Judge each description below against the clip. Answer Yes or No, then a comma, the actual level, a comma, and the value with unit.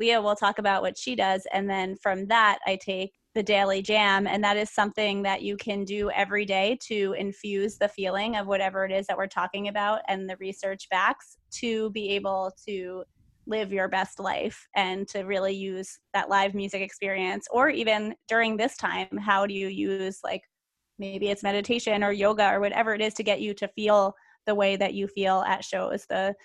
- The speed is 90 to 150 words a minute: No, fast, 205 wpm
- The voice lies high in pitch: Yes, high, 200 Hz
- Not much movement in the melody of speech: Yes, narrow, 1.3 semitones